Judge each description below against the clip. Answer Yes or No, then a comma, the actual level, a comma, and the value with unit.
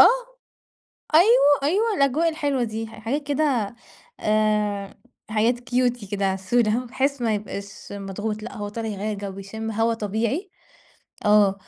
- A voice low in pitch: No, high, 220 Hz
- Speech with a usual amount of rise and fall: Yes, average, 3.6 semitones